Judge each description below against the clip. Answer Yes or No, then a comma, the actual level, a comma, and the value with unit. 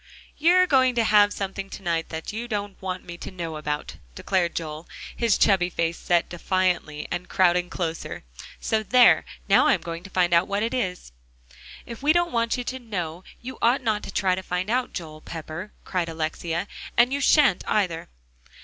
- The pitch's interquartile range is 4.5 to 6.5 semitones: Yes, average, 5.2 semitones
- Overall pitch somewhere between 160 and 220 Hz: Yes, medium, 185 Hz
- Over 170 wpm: Yes, average, 190 wpm